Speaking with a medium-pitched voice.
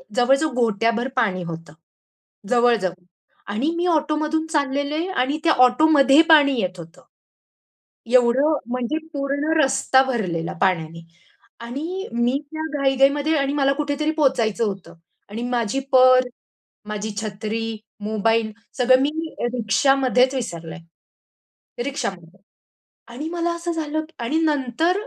No: very high, 260 Hz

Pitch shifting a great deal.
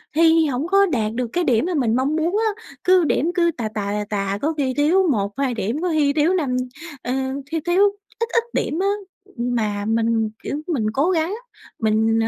Yes: wide, 7.1 semitones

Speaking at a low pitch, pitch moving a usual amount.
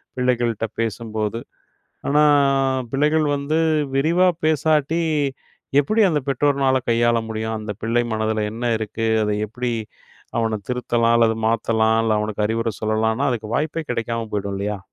Yes: low, 115 Hz; average, 3.8 semitones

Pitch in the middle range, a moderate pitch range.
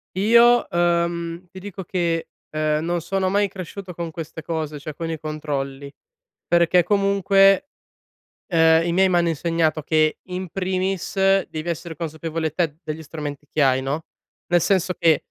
Yes: medium, 170 Hz; average, 3.0 semitones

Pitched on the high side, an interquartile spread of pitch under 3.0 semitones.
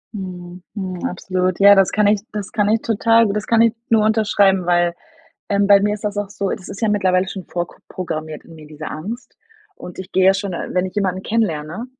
Yes: high, 195 Hz; narrow, 2.6 semitones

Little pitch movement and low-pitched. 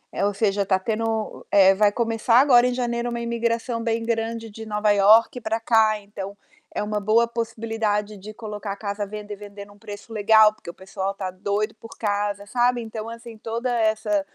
No: narrow, 2.0 semitones; high, 215 Hz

